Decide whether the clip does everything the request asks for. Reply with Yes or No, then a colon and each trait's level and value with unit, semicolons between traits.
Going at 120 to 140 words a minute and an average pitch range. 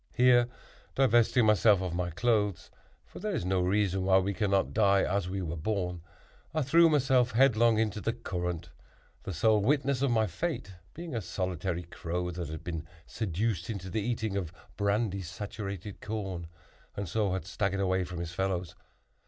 No: average, 170 wpm; average, 3.8 semitones